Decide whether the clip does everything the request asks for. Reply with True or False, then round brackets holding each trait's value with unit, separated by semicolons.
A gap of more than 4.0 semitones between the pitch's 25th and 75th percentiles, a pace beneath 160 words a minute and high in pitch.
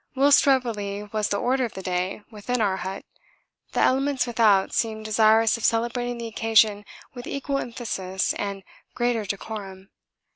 False (3.3 semitones; 150 wpm; 220 Hz)